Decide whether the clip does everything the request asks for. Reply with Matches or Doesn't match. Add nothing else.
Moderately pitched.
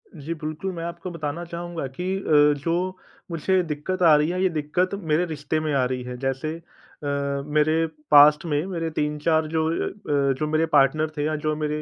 Matches